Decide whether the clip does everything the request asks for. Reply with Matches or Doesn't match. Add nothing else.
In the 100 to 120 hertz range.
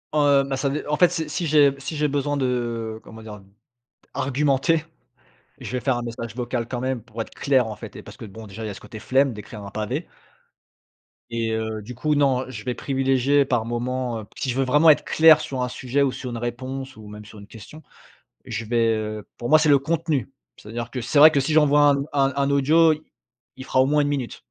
Doesn't match